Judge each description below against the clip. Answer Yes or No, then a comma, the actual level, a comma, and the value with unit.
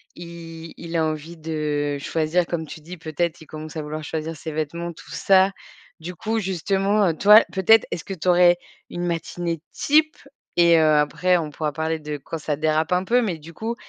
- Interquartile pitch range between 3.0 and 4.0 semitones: No, narrow, 2.5 semitones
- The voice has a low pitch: No, medium, 165 Hz